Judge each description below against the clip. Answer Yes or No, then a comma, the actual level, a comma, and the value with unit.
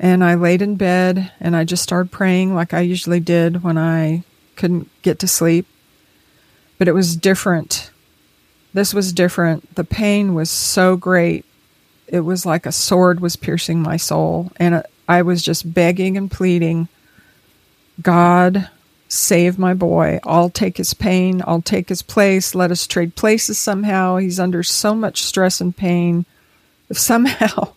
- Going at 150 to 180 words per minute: Yes, average, 160 wpm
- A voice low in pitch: No, medium, 180 Hz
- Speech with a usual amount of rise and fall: No, narrow, 1.7 semitones